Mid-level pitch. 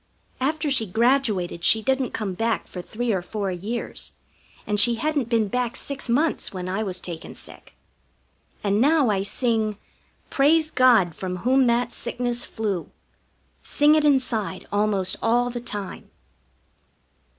No: high, 230 Hz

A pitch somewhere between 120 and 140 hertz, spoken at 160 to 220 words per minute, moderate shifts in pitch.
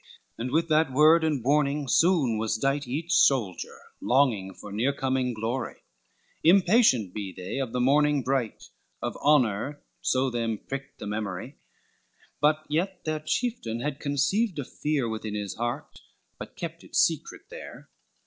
No: low, 135 Hz; average, 150 wpm; average, 5.0 semitones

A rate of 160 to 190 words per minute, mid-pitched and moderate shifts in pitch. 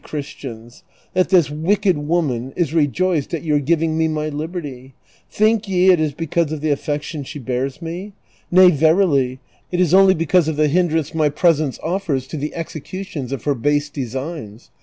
Yes: average, 175 wpm; medium, 155 Hz; average, 3.5 semitones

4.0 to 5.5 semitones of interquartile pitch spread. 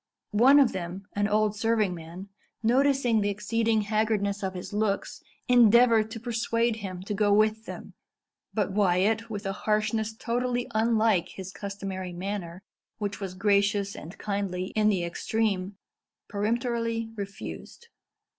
No: narrow, 2.5 semitones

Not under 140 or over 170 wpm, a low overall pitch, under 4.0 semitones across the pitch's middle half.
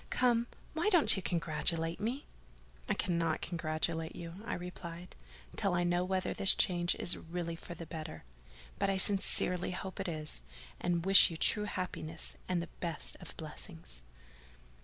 No: average, 160 wpm; medium, 175 Hz; narrow, 2.4 semitones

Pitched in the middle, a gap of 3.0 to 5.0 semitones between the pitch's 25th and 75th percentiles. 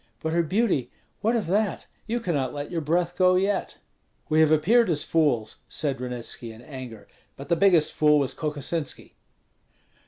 Yes: medium, 155 Hz; average, 4.6 semitones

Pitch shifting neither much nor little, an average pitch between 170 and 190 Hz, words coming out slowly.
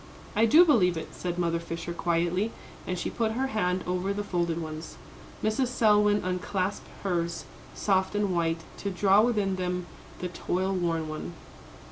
No: average, 3.2 semitones; medium, 185 Hz; average, 160 wpm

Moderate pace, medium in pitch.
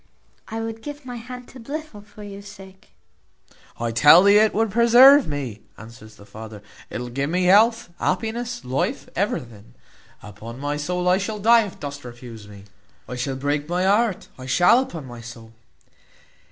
Yes: average, 175 wpm; medium, 180 Hz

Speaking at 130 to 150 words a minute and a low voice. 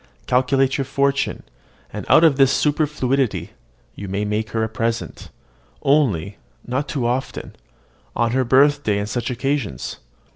Yes: average, 140 wpm; low, 130 Hz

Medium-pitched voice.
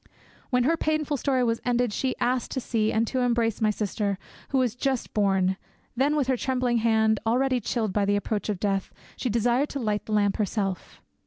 No: high, 230 Hz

